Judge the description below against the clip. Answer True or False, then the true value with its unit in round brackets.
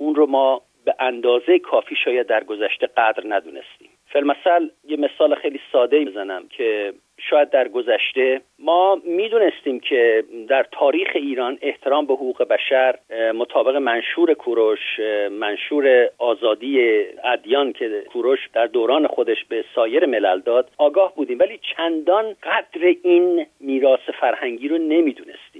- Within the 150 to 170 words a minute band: False (130 wpm)